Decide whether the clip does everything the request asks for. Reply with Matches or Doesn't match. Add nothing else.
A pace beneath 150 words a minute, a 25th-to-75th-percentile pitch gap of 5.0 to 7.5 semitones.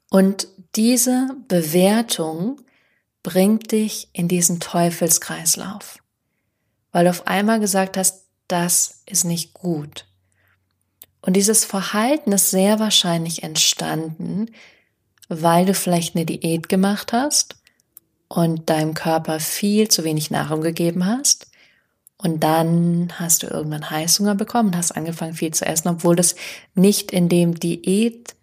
Doesn't match